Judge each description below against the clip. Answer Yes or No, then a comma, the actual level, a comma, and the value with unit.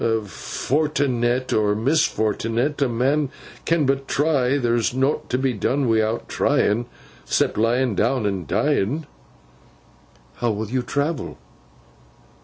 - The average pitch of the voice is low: Yes, low, 125 Hz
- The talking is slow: Yes, slow, 110 wpm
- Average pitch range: Yes, average, 3.7 semitones